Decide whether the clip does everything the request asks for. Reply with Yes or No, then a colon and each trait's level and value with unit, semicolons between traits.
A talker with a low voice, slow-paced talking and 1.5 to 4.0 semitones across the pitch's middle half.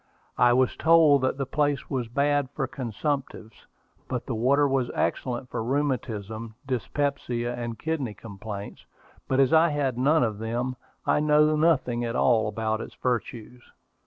No: low, 125 Hz; average, 155 wpm; average, 3.7 semitones